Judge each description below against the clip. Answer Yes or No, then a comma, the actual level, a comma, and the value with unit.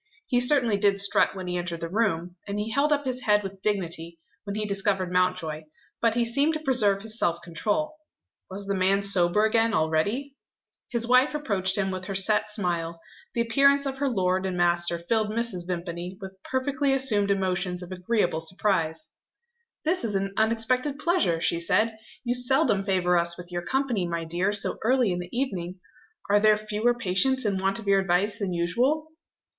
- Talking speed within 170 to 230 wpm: Yes, average, 185 wpm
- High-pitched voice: Yes, high, 200 Hz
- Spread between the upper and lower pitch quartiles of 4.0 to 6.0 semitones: Yes, average, 4.8 semitones